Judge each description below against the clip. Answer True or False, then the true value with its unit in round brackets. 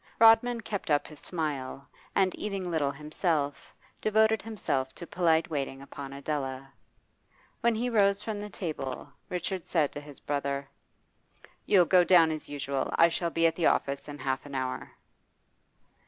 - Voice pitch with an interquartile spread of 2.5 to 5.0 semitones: False (5.6 semitones)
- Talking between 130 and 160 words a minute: True (155 wpm)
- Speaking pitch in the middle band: True (160 Hz)